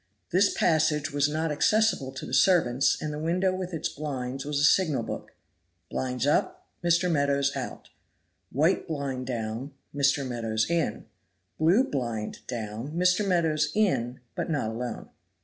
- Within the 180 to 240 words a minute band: No, average, 150 wpm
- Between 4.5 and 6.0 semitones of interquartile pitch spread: Yes, average, 4.9 semitones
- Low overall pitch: No, medium, 145 Hz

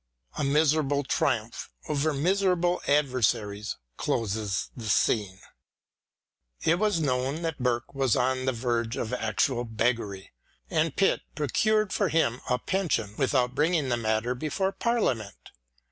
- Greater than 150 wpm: No, slow, 135 wpm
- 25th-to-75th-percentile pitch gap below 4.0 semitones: No, wide, 5.5 semitones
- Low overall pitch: Yes, low, 130 Hz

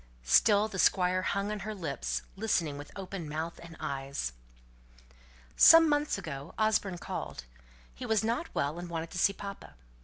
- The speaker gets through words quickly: No, average, 160 wpm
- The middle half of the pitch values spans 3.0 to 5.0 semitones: No, wide, 5.4 semitones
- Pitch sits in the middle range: Yes, medium, 180 Hz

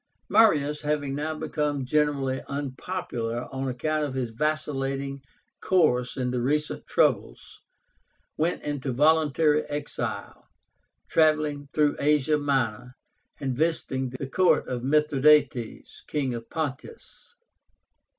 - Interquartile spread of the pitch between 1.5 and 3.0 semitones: Yes, narrow, 2.6 semitones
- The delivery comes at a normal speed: No, slow, 110 wpm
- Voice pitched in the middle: Yes, medium, 145 Hz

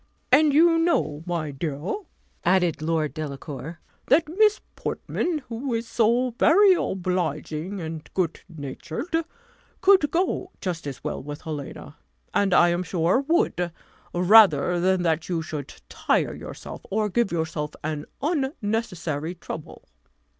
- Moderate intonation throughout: No, wide, 7.9 semitones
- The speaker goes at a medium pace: No, slow, 130 wpm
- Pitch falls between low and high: Yes, medium, 180 Hz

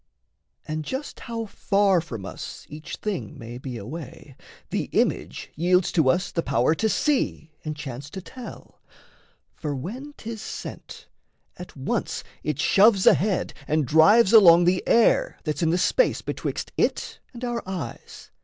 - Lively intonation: Yes, wide, 6.2 semitones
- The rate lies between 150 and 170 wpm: Yes, average, 155 wpm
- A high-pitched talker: No, medium, 175 Hz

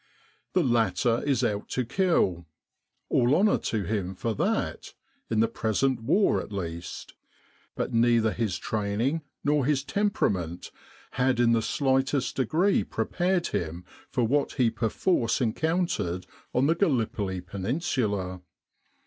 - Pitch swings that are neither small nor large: No, wide, 5.9 semitones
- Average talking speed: No, slow, 130 wpm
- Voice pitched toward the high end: No, low, 120 Hz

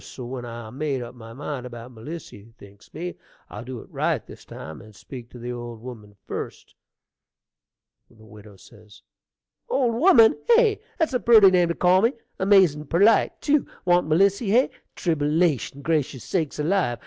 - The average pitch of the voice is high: No, medium, 150 Hz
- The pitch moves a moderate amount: No, wide, 8.1 semitones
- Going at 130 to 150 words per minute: No, average, 160 wpm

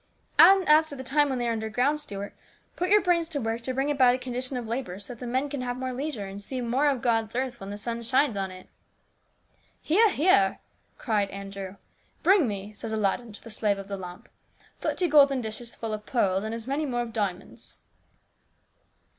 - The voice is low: No, high, 240 Hz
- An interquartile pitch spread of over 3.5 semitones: Yes, average, 4.9 semitones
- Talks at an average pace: No, fast, 230 wpm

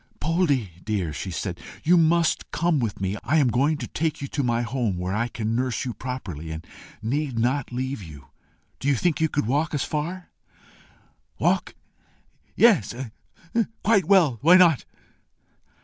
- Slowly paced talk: No, average, 165 wpm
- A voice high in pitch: No, low, 130 Hz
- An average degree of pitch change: No, wide, 6.4 semitones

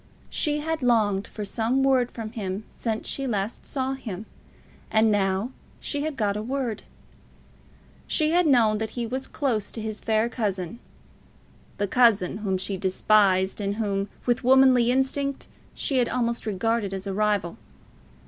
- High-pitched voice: Yes, high, 220 Hz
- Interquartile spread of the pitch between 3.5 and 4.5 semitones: Yes, average, 4.1 semitones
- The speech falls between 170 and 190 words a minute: No, average, 160 wpm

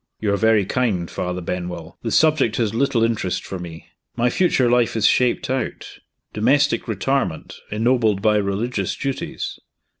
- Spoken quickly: No, average, 150 wpm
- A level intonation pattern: No, average, 4.3 semitones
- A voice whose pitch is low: Yes, low, 110 Hz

